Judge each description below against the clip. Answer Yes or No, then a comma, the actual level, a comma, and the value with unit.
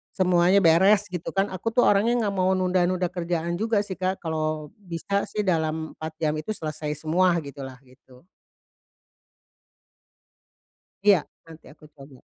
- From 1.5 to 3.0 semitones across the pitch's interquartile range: No, average, 3.4 semitones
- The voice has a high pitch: No, medium, 175 Hz